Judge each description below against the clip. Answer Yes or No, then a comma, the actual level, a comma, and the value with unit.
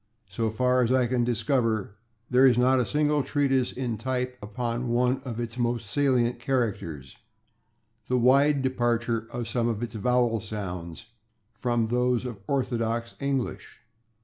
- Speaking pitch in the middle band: No, low, 120 Hz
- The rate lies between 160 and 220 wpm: No, average, 150 wpm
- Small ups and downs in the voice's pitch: Yes, narrow, 2.0 semitones